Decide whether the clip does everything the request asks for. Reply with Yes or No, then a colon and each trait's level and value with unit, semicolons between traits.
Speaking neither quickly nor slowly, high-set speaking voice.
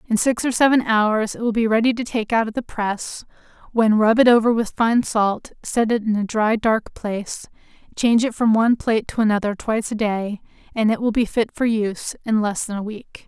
No: fast, 230 wpm; high, 220 Hz